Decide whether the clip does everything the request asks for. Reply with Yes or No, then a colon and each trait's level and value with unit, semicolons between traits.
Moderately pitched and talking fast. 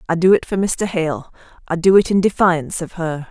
Yes: medium, 175 Hz; fast, 235 wpm